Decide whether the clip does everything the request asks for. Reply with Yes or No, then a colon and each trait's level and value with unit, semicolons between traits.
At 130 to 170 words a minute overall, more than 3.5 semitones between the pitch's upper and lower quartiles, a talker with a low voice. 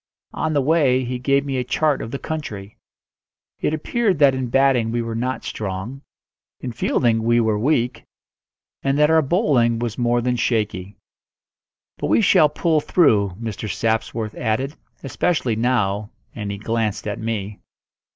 Yes: average, 160 wpm; average, 3.9 semitones; low, 120 Hz